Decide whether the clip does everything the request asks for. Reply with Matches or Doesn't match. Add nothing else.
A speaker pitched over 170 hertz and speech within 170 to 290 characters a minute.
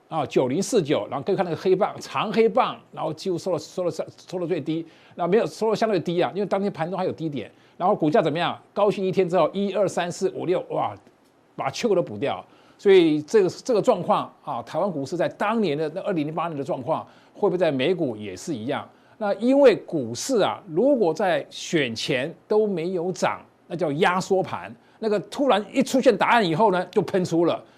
Doesn't match